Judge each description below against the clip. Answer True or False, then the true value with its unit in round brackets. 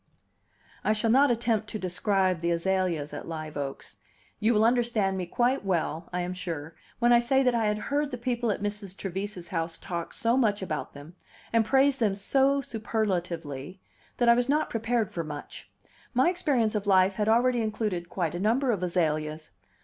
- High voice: True (205 Hz)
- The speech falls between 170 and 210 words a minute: True (190 wpm)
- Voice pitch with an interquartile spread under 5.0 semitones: False (5.4 semitones)